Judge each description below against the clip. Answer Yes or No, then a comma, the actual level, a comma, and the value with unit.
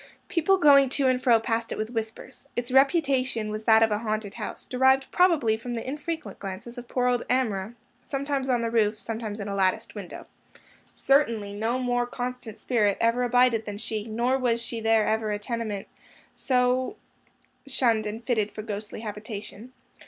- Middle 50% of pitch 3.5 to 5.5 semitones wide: No, average, 2.9 semitones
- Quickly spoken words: No, average, 175 wpm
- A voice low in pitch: No, high, 230 Hz